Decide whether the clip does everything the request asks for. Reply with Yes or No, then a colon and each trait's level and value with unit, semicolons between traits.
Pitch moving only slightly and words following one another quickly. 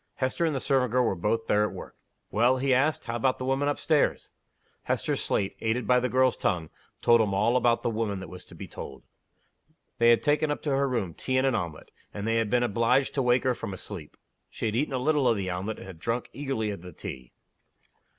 No: average, 4.1 semitones; fast, 245 wpm